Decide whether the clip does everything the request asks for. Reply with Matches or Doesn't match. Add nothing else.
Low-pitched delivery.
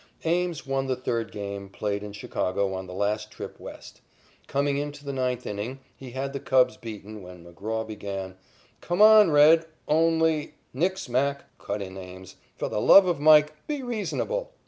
Matches